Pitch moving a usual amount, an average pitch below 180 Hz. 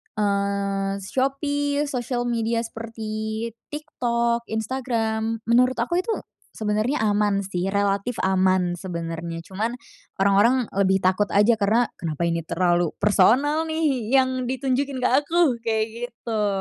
No: average, 4.2 semitones; high, 220 Hz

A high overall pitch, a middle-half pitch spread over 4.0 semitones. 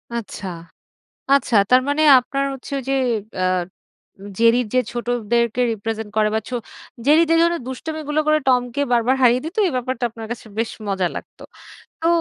No: high, 245 Hz; average, 3.7 semitones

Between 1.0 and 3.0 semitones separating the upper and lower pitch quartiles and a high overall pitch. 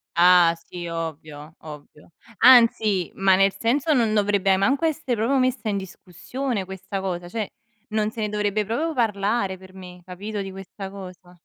No: average, 3.6 semitones; high, 195 Hz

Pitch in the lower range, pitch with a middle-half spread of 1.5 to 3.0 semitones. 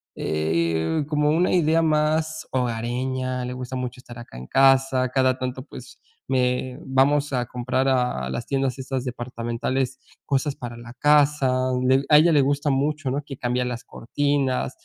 Yes: low, 130 Hz; narrow, 2.4 semitones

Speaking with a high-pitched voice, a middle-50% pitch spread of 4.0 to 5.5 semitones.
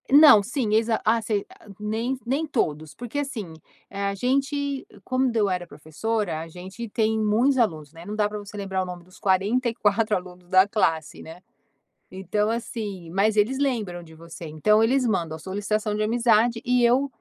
Yes: high, 210 Hz; average, 4.3 semitones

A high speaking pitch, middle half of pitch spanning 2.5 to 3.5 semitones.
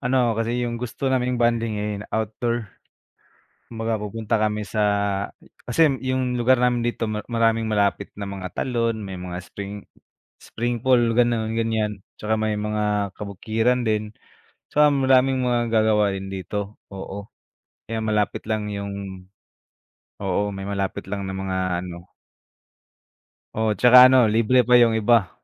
No: low, 110 Hz; average, 2.8 semitones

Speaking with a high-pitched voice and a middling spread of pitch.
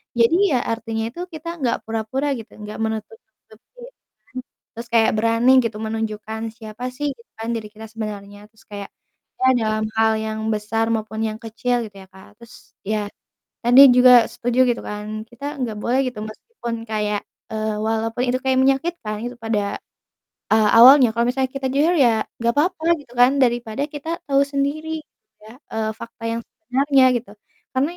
Yes: high, 230 Hz; average, 3.3 semitones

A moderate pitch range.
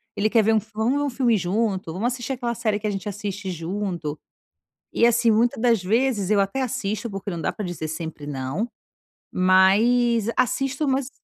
Yes: average, 4.1 semitones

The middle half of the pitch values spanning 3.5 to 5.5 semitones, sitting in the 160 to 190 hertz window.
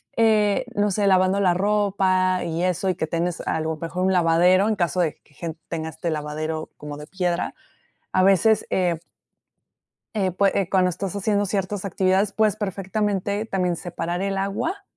No: average, 2.8 semitones; medium, 185 Hz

